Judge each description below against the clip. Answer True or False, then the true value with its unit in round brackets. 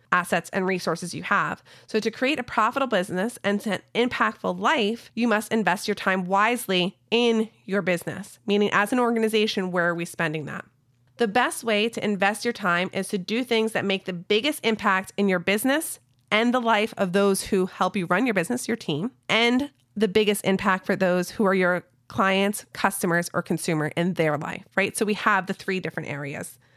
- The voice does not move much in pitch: False (3.7 semitones)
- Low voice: False (200 Hz)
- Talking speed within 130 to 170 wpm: False (200 wpm)